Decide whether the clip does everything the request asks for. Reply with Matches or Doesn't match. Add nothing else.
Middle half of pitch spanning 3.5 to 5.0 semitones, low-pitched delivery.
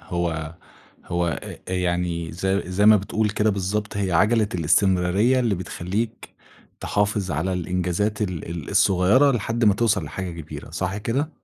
Doesn't match